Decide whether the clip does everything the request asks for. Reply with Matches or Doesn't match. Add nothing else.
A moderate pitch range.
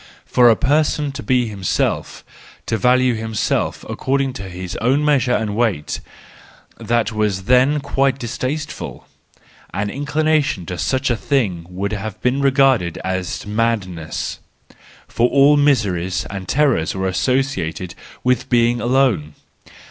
Doesn't match